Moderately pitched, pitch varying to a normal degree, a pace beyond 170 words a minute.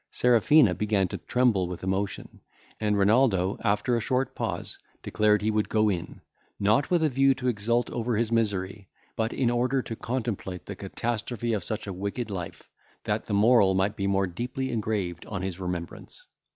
No: low, 105 Hz; average, 3.7 semitones; average, 180 wpm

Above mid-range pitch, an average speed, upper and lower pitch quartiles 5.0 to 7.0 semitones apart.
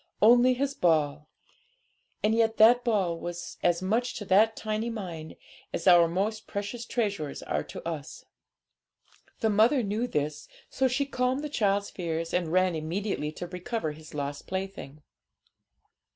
Yes: high, 195 Hz; average, 150 wpm; wide, 5.4 semitones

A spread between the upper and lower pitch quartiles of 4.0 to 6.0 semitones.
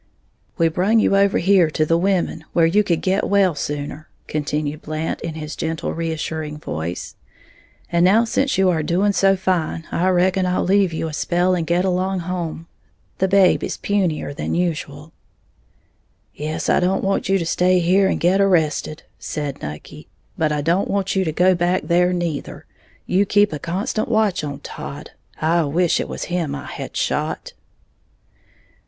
No: average, 3.3 semitones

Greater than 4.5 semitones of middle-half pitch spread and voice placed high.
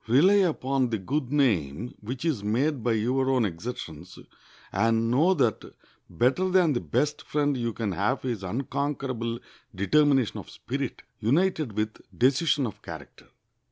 No: average, 4.9 semitones; low, 125 Hz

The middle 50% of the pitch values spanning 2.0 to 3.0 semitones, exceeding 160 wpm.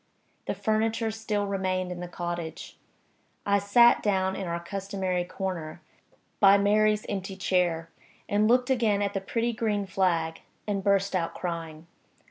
No: average, 2.7 semitones; average, 145 wpm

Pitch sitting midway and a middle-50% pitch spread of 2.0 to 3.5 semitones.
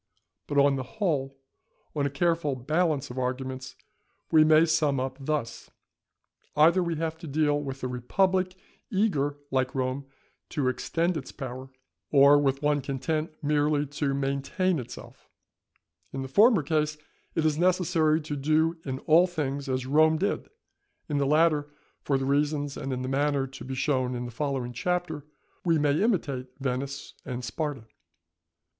Yes: medium, 145 Hz; average, 2.9 semitones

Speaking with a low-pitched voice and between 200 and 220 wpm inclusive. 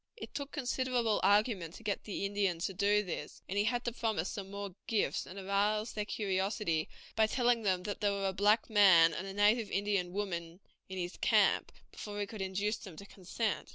No: high, 205 Hz; fast, 205 wpm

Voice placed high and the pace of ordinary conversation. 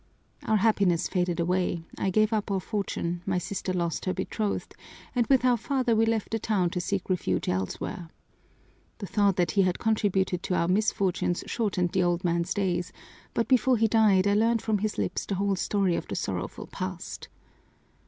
Yes: high, 195 Hz; average, 185 wpm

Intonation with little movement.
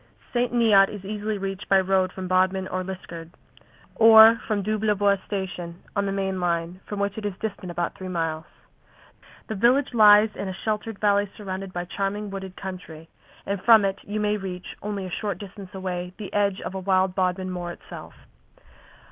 Yes: narrow, 2.0 semitones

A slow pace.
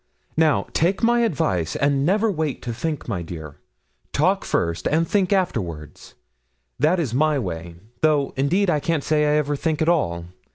No: average, 170 wpm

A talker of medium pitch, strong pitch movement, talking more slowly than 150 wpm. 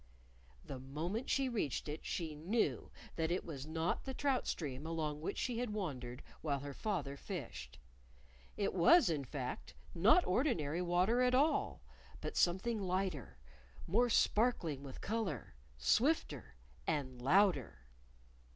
Yes: medium, 170 Hz; wide, 7.6 semitones; slow, 135 wpm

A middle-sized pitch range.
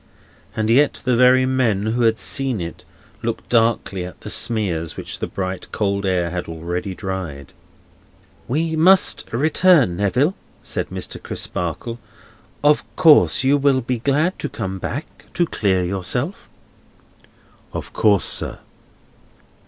No: wide, 6.7 semitones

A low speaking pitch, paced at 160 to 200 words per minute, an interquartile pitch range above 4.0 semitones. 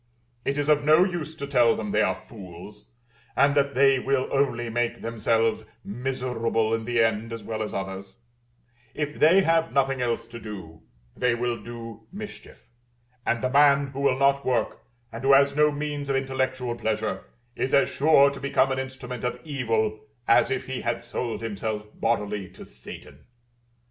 No: low, 125 Hz; average, 175 wpm; average, 3.6 semitones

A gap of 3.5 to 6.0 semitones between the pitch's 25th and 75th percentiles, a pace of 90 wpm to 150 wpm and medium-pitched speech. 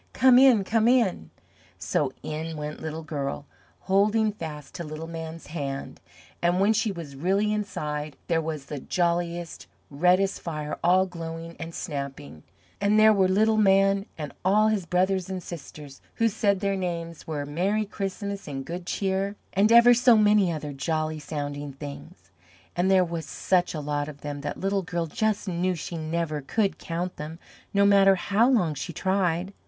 No: average, 4.4 semitones; average, 170 wpm; medium, 175 Hz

